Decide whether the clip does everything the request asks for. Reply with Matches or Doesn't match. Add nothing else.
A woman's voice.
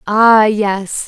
Matches